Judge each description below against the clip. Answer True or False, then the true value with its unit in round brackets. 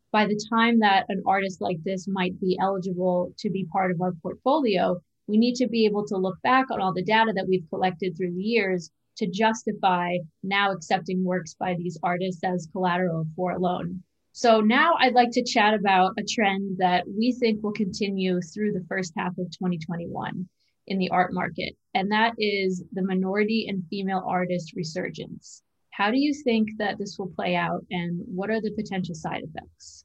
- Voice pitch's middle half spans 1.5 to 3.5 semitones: True (2.7 semitones)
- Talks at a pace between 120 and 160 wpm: False (195 wpm)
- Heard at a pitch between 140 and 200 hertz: True (190 Hz)